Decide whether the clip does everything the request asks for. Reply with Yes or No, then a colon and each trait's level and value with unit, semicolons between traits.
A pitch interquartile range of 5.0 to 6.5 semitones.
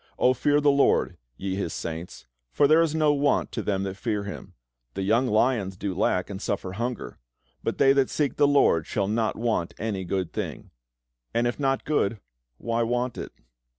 Yes: wide, 5.6 semitones